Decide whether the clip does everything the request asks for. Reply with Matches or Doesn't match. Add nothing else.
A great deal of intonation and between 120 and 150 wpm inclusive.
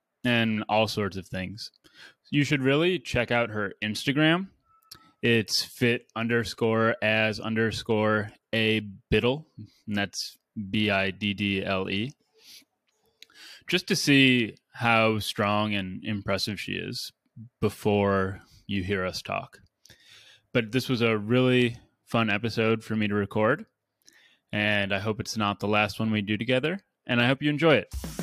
Doesn't match